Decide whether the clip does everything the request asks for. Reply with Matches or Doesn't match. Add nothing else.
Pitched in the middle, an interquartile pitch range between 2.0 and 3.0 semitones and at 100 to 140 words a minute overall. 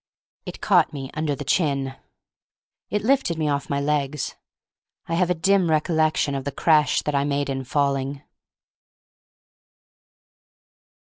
Matches